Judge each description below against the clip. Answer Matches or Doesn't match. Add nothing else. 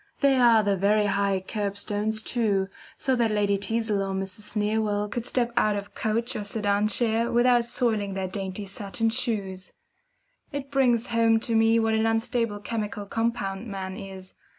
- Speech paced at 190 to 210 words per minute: Doesn't match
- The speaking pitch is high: Matches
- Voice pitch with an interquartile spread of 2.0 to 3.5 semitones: Matches